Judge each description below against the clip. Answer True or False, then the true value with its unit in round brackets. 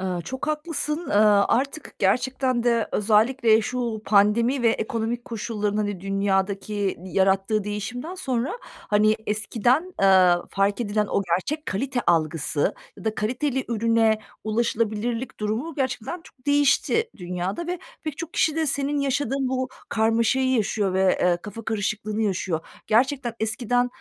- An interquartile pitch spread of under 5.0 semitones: True (4.3 semitones)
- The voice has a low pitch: False (225 Hz)